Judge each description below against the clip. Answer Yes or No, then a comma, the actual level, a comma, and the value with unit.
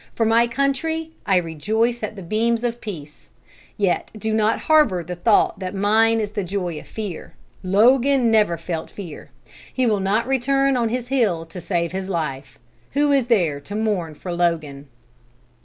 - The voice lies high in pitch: Yes, high, 210 Hz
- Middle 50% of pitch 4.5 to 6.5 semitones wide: Yes, average, 5.2 semitones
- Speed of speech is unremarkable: Yes, average, 175 wpm